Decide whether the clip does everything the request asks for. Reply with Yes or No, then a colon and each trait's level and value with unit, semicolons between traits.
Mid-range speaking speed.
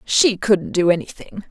Yes: average, 160 wpm